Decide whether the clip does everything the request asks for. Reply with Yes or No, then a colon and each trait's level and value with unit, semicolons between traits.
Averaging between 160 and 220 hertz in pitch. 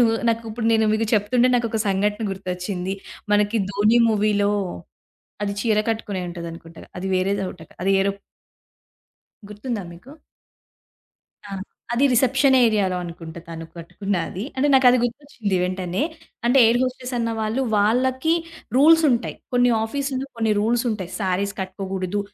Yes: high, 210 Hz